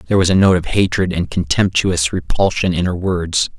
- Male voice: Yes, male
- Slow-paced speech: No, average, 200 wpm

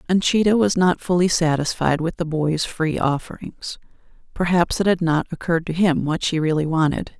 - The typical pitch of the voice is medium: Yes, medium, 165 Hz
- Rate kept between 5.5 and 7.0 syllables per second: No, 5.2 syllables/s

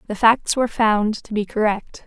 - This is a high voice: Yes, high, 220 Hz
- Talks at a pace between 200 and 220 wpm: Yes, fast, 205 wpm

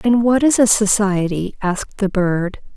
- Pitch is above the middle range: Yes, high, 205 Hz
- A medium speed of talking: Yes, average, 175 wpm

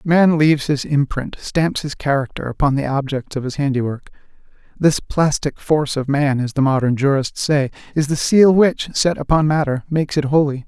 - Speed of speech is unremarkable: Yes, average, 185 wpm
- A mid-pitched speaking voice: Yes, medium, 145 Hz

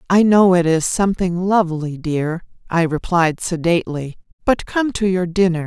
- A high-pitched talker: No, medium, 175 Hz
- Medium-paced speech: Yes, average, 160 wpm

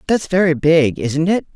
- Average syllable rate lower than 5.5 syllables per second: Yes, 4.6 syllables/s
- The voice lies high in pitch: No, medium, 160 Hz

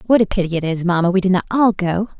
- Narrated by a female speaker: Yes, female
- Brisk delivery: Yes, fast, 300 wpm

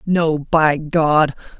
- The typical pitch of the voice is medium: Yes, medium, 155 Hz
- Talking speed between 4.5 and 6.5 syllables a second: No, 2.4 syllables/s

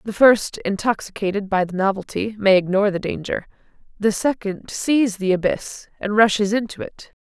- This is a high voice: Yes, high, 205 Hz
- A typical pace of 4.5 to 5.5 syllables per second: Yes, 5.0 syllables/s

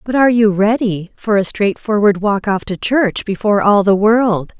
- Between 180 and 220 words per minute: Yes, average, 185 wpm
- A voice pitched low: No, high, 205 Hz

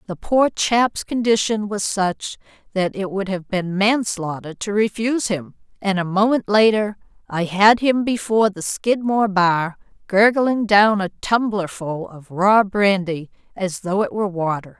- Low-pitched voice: No, high, 200 Hz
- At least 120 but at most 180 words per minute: Yes, average, 155 wpm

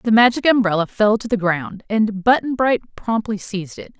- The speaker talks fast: No, average, 195 wpm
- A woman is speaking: Yes, female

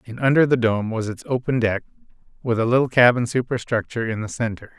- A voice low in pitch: Yes, low, 120 Hz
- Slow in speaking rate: No, average, 200 wpm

